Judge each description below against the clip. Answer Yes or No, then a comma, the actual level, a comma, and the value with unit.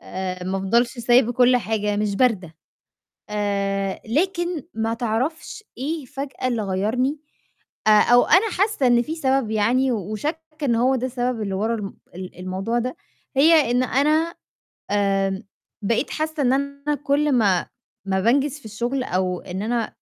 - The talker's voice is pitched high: Yes, high, 240 Hz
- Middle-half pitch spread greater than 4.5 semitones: Yes, average, 5.2 semitones